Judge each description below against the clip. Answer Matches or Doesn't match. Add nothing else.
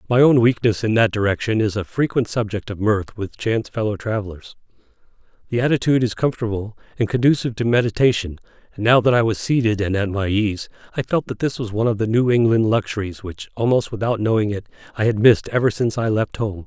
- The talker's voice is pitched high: Doesn't match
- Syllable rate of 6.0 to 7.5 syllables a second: Matches